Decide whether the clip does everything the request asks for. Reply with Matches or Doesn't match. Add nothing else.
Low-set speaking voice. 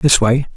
Matches